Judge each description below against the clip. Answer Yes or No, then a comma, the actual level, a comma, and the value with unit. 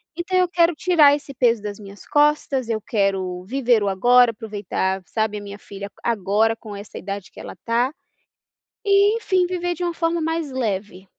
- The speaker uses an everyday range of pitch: No, wide, 8.1 semitones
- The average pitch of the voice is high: Yes, high, 235 Hz